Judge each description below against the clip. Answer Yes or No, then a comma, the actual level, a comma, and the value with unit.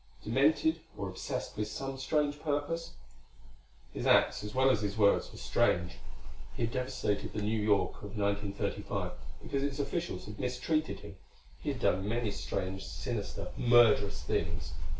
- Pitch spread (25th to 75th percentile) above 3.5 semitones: Yes, average, 5.2 semitones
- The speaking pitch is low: Yes, low, 110 Hz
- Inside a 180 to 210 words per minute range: No, average, 150 wpm